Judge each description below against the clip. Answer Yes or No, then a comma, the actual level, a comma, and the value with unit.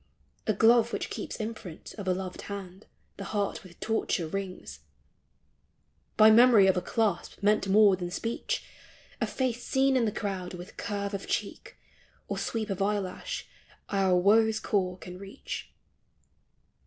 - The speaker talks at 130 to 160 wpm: Yes, average, 150 wpm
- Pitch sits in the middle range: No, high, 200 Hz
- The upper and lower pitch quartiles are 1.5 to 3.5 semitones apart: Yes, average, 3.0 semitones